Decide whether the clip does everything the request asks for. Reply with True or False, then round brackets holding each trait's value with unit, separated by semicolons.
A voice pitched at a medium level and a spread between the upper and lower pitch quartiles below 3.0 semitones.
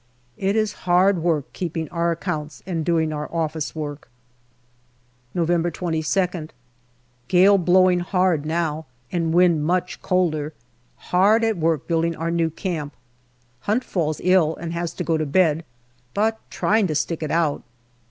True (170 Hz; 2.5 semitones)